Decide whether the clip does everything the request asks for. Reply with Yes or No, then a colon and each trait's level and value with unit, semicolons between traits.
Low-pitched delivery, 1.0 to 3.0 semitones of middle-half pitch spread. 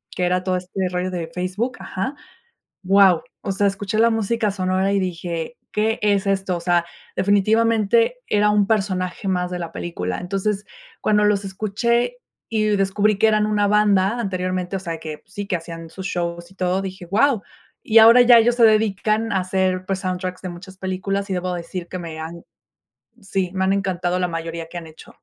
No: high, 190 Hz; narrow, 2.6 semitones